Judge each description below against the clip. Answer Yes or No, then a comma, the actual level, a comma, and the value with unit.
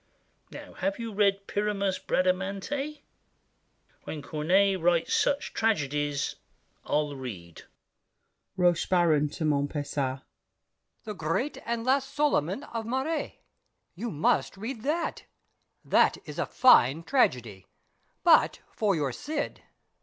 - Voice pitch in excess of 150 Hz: Yes, high, 190 Hz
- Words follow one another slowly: Yes, slow, 105 wpm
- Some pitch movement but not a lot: No, wide, 8.0 semitones